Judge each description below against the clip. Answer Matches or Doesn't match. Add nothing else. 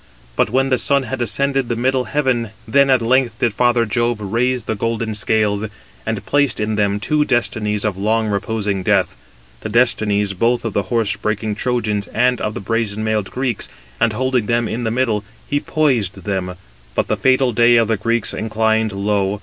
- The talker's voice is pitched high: Doesn't match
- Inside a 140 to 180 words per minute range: Doesn't match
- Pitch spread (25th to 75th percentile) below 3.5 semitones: Matches